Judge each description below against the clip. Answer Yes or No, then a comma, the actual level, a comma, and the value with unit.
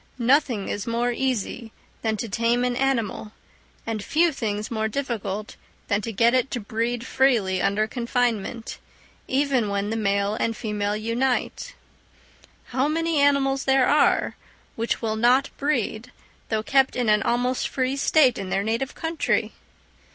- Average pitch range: Yes, average, 3.6 semitones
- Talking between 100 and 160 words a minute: Yes, average, 150 wpm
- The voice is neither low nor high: No, high, 235 Hz